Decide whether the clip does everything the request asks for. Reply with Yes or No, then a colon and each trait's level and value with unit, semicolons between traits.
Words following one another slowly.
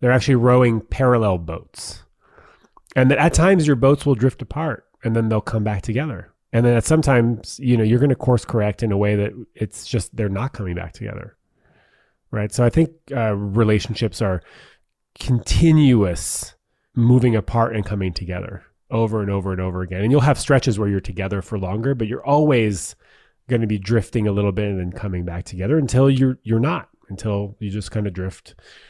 No: average, 195 wpm